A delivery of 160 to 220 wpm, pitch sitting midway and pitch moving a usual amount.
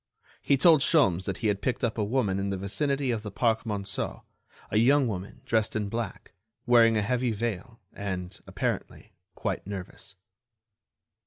No: average, 165 wpm; low, 110 Hz; average, 3.7 semitones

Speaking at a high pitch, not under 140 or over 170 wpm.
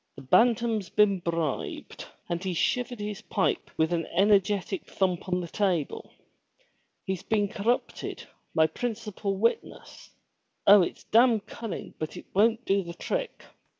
Yes: high, 200 Hz; average, 150 wpm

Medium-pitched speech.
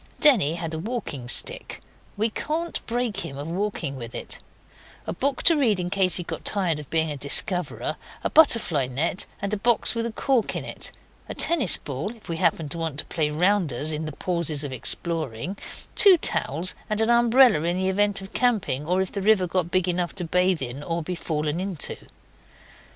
Yes: medium, 180 Hz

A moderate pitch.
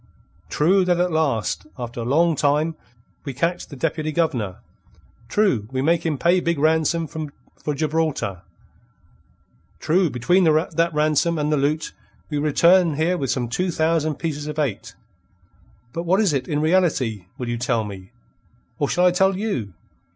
Yes: medium, 155 Hz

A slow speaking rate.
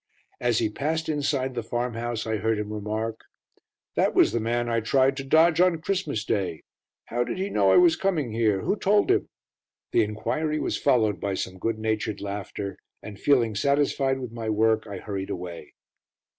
No: average, 185 wpm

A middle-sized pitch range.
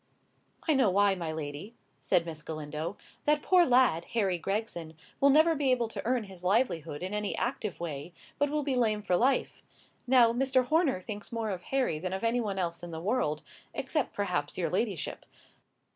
No: wide, 6.8 semitones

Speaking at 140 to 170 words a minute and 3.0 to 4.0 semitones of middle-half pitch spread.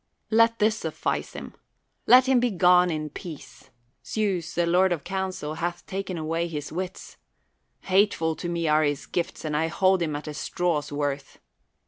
Yes: average, 165 wpm; average, 3.5 semitones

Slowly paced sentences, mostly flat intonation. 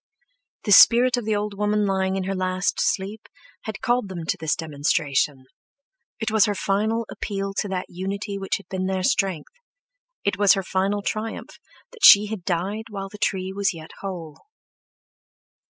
No: average, 170 wpm; narrow, 2.2 semitones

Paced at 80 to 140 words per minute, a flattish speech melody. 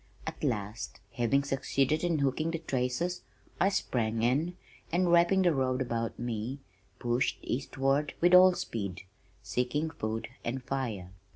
No: slow, 135 wpm; wide, 5.5 semitones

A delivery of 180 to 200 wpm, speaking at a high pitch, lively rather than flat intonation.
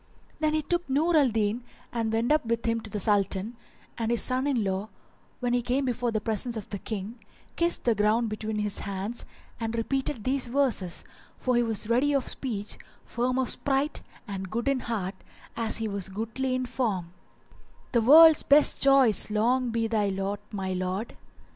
No: average, 185 wpm; high, 230 Hz; average, 3.6 semitones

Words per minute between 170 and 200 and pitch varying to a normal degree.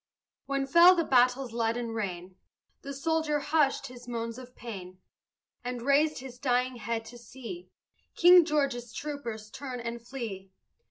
No: average, 145 wpm; average, 3.3 semitones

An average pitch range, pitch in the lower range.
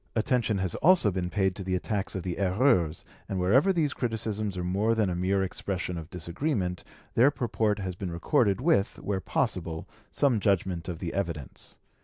Yes: average, 3.8 semitones; very low, 95 Hz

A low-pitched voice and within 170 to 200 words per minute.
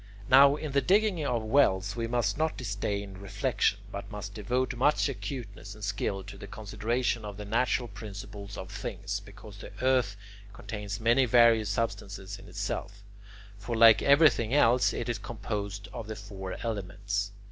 No: low, 105 Hz; average, 160 wpm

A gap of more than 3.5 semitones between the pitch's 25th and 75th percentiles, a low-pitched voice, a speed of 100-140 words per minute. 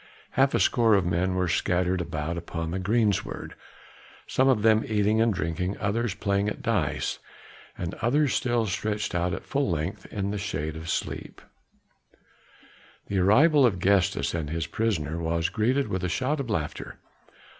No: average, 4.7 semitones; low, 100 Hz; average, 160 wpm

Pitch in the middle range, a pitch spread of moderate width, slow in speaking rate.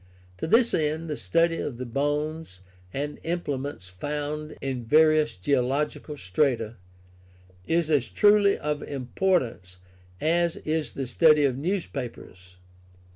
Yes: medium, 150 Hz; average, 4.2 semitones; slow, 120 wpm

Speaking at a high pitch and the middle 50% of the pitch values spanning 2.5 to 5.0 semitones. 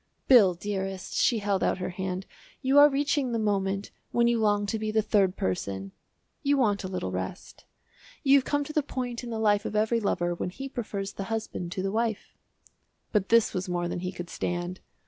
Yes: high, 205 Hz; average, 4.2 semitones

